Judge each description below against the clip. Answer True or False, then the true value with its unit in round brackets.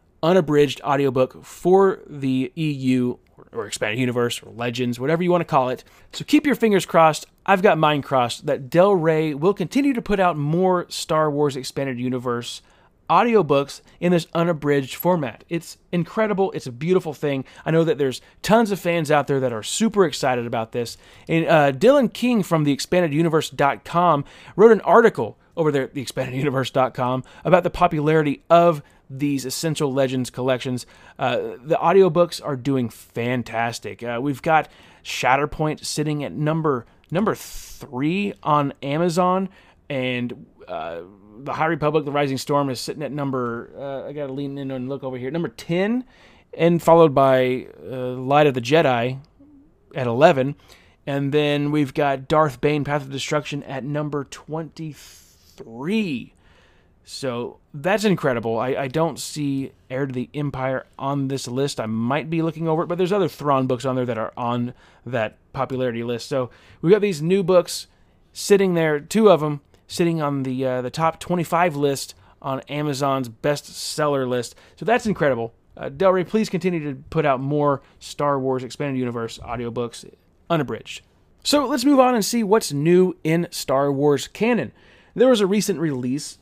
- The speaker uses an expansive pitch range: False (4.8 semitones)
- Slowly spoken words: False (170 wpm)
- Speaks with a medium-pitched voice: True (145 Hz)